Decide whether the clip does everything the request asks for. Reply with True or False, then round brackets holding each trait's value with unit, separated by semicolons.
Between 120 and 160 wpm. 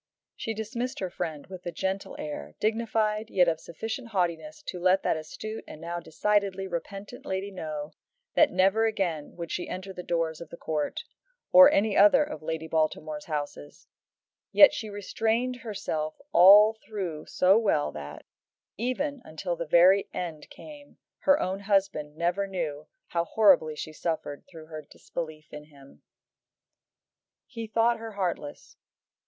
True (150 wpm)